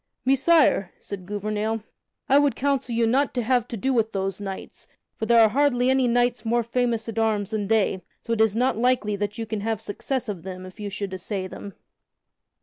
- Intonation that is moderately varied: Yes, average, 3.3 semitones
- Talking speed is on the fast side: Yes, fast, 210 wpm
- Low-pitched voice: No, high, 225 Hz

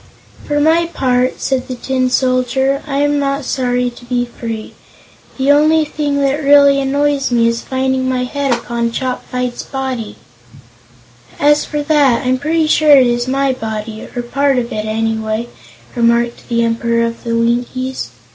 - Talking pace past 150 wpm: Yes, average, 165 wpm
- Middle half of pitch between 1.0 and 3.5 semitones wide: Yes, average, 2.9 semitones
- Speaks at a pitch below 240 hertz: No, very high, 255 Hz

